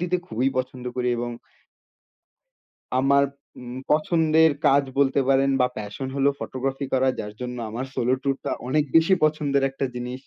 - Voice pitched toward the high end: No, low, 135 Hz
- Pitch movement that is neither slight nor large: No, narrow, 2.1 semitones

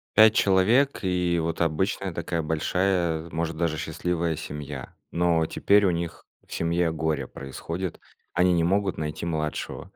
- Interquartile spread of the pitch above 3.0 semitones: No, narrow, 2.4 semitones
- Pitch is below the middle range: Yes, very low, 85 Hz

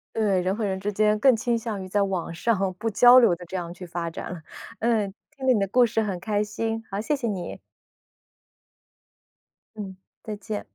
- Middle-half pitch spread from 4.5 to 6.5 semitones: No, average, 3.0 semitones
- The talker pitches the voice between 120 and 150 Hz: No, high, 210 Hz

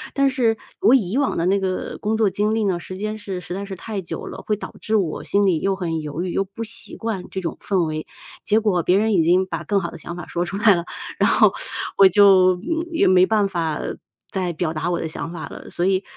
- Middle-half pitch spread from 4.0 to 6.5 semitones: No, average, 3.3 semitones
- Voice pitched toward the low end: No, high, 190 Hz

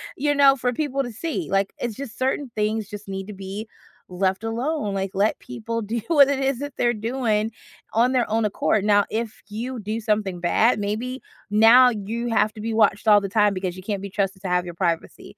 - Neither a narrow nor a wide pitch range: Yes, average, 3.5 semitones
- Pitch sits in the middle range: No, high, 215 Hz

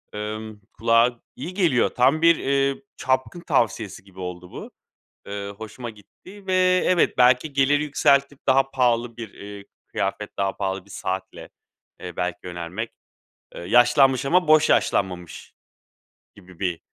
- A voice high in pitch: No, low, 120 Hz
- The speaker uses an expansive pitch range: Yes, wide, 5.8 semitones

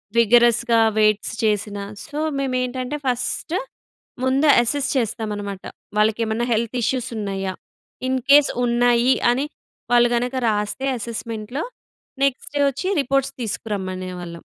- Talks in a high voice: Yes, high, 235 Hz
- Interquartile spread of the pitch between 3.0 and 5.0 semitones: Yes, average, 3.5 semitones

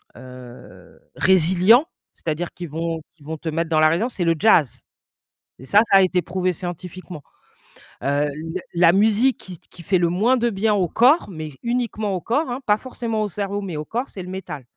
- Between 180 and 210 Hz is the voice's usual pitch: Yes, medium, 185 Hz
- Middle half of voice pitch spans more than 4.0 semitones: Yes, average, 4.6 semitones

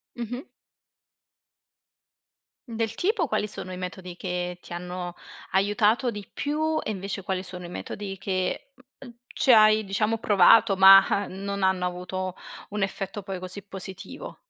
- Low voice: No, high, 195 Hz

